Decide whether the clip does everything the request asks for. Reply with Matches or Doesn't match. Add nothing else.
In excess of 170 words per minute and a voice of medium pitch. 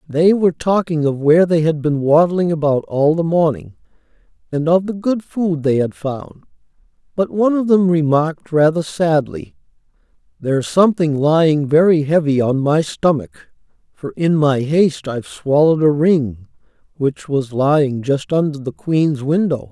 Doesn't match